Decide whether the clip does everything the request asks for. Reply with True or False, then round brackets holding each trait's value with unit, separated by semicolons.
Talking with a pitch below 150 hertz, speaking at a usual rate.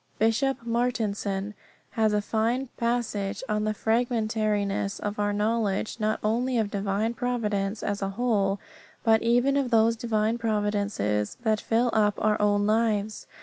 False (215 Hz; 145 wpm)